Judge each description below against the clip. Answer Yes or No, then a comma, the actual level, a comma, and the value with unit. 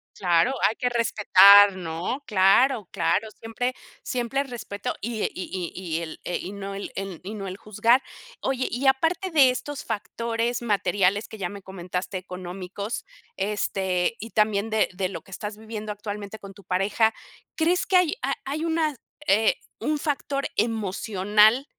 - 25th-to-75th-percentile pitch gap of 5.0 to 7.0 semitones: No, average, 4.2 semitones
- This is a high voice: Yes, high, 210 Hz